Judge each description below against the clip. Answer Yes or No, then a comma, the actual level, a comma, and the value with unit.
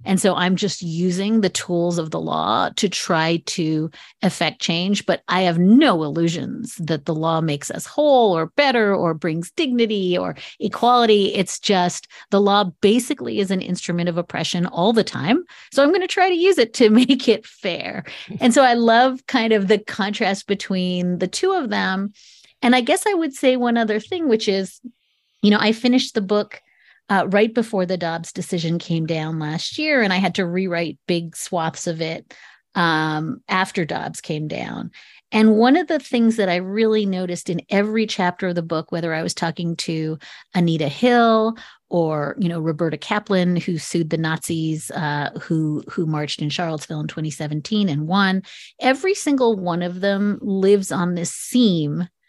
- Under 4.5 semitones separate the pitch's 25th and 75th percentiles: No, average, 4.9 semitones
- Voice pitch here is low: No, medium, 185 Hz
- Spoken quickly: No, average, 185 wpm